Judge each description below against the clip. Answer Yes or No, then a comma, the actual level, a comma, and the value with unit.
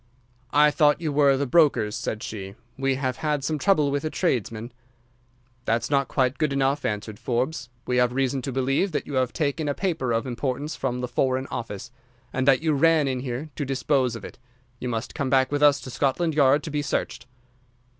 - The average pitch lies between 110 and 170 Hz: Yes, low, 135 Hz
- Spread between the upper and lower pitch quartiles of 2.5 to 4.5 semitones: Yes, average, 2.8 semitones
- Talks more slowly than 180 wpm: No, fast, 205 wpm